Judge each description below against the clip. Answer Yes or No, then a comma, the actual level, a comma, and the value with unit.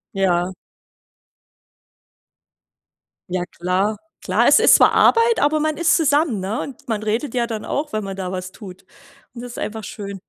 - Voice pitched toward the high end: Yes, high, 215 Hz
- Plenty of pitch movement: Yes, wide, 6.8 semitones